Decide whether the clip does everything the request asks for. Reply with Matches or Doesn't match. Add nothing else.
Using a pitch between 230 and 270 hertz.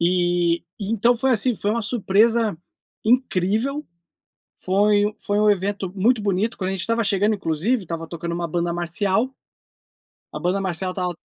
Doesn't match